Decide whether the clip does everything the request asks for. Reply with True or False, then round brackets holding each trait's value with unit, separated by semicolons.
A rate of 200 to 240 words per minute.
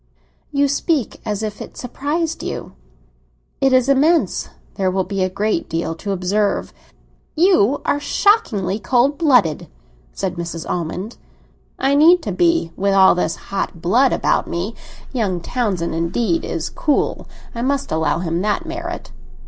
False (150 wpm)